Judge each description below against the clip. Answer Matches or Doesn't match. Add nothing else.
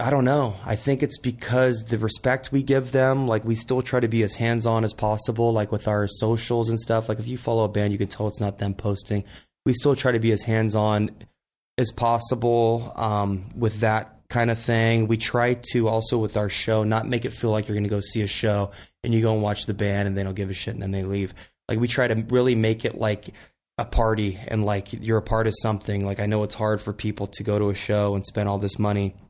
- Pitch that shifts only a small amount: Matches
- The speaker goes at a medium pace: Doesn't match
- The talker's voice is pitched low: Matches